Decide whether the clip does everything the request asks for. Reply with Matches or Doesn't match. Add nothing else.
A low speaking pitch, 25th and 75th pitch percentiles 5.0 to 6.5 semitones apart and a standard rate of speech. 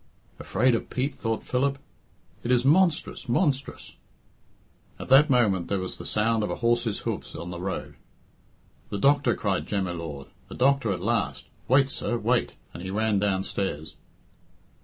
Matches